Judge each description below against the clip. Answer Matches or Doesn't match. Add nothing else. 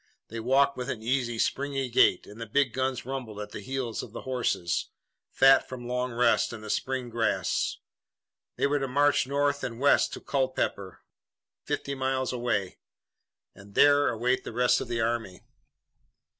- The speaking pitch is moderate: Doesn't match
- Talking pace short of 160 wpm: Doesn't match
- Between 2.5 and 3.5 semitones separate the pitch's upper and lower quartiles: Matches